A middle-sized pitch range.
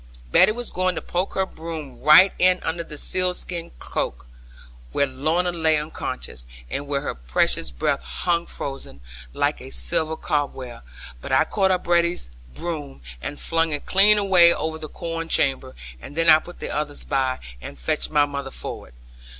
Yes: average, 4.2 semitones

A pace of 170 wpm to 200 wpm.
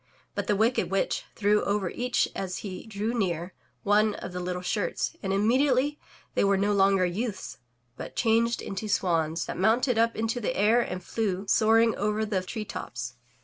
Yes: average, 180 wpm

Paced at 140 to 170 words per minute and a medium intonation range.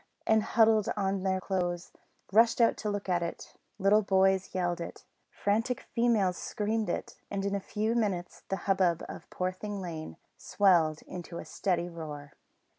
Yes: average, 160 wpm; average, 3.0 semitones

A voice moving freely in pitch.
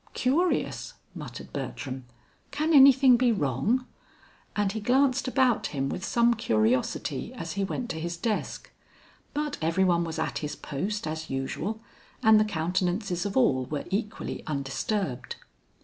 Yes: wide, 7.8 semitones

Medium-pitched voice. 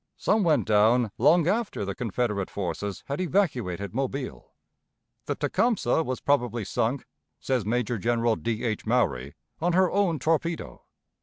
No: low, 125 Hz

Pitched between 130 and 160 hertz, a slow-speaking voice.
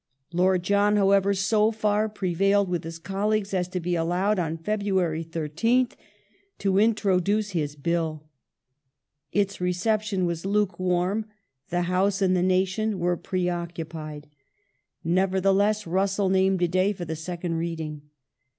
No: medium, 185 Hz; slow, 130 wpm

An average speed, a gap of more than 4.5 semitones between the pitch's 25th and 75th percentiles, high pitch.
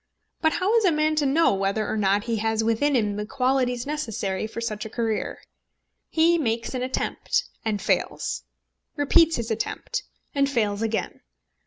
Yes: average, 170 wpm; average, 5.3 semitones; high, 235 Hz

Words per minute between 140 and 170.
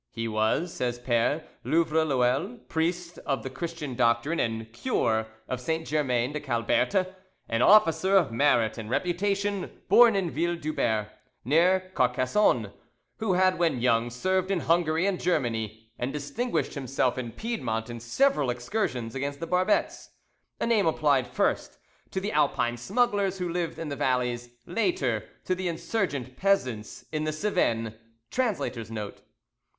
Yes: average, 145 wpm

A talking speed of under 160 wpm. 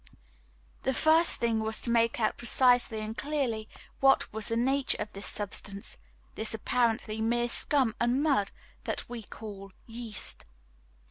Yes: average, 145 wpm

